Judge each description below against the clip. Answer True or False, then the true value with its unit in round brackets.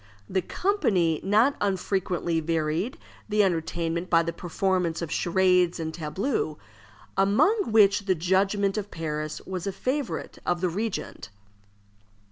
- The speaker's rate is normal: False (125 wpm)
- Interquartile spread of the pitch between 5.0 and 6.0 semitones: False (3.4 semitones)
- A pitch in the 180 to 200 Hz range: True (185 Hz)